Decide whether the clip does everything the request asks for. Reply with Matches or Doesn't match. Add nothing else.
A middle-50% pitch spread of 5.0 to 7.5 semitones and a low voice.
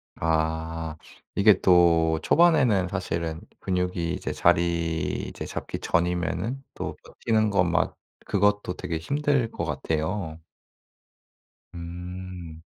Doesn't match